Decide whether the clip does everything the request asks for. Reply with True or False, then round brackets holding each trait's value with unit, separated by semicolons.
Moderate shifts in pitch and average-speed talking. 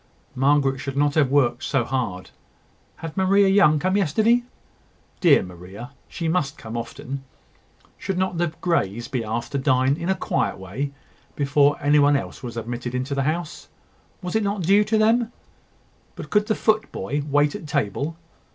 False (6.0 semitones; 170 wpm)